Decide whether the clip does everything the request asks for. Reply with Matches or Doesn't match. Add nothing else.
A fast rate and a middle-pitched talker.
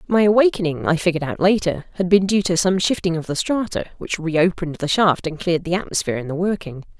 Matches